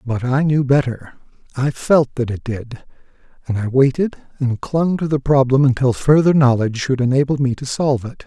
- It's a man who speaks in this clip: Yes, male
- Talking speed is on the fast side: No, average, 190 wpm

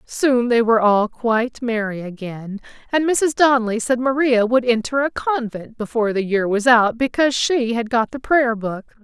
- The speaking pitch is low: No, high, 235 Hz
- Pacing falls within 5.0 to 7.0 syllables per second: No, 4.8 syllables/s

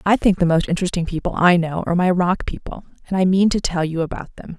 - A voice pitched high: No, medium, 175 Hz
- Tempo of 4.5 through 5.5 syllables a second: No, 6.4 syllables/s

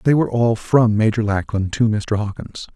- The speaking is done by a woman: No, male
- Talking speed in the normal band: Yes, average, 195 wpm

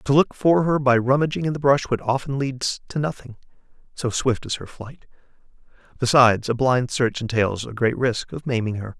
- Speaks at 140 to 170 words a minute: No, average, 195 wpm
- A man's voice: Yes, male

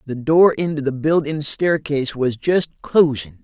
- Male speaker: Yes, male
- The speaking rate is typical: Yes, average, 155 wpm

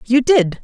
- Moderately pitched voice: No, very high, 250 Hz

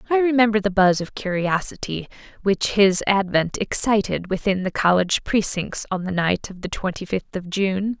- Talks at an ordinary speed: Yes, average, 175 wpm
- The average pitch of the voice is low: No, high, 195 Hz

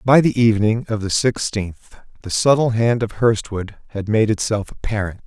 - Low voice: Yes, low, 110 Hz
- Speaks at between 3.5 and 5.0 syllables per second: Yes, 4.9 syllables/s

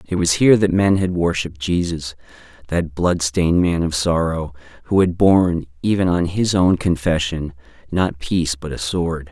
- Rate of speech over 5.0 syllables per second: No, 4.9 syllables/s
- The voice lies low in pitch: Yes, very low, 85 Hz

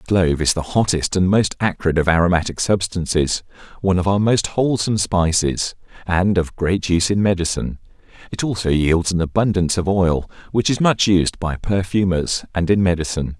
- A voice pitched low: Yes, very low, 90 Hz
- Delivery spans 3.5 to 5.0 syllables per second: No, 5.5 syllables/s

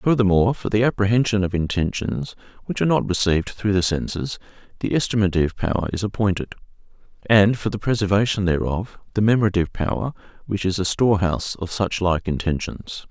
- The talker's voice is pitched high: No, low, 100 Hz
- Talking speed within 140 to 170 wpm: Yes, average, 155 wpm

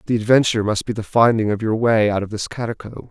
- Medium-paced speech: No, fast, 250 wpm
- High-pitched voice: No, low, 110 Hz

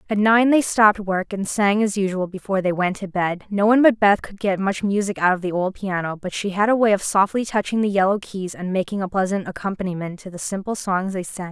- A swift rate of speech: Yes, fast, 255 wpm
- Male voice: No, female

